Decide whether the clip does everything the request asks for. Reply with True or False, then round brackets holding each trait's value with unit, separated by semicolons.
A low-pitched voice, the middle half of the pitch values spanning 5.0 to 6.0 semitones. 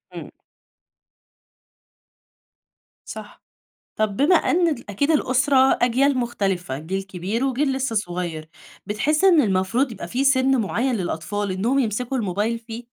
False (230 Hz; 5.6 semitones)